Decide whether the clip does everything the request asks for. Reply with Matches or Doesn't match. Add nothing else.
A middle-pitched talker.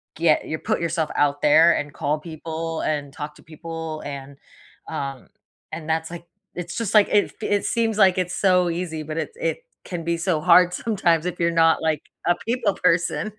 Matches